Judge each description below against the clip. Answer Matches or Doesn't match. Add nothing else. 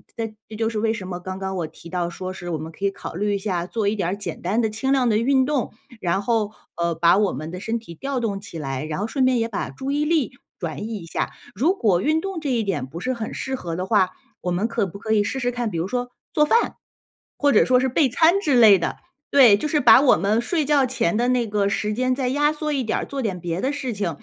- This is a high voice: Matches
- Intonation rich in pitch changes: Matches